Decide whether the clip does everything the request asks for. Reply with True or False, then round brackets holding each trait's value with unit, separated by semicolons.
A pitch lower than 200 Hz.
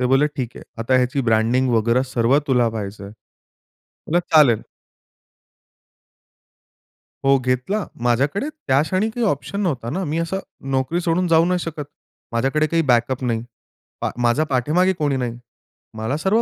True (135 Hz)